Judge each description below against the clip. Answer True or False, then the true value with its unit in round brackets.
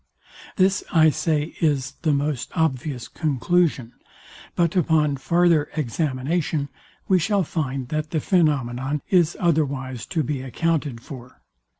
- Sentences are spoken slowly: True (120 wpm)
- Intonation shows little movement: False (3.9 semitones)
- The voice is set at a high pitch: False (150 Hz)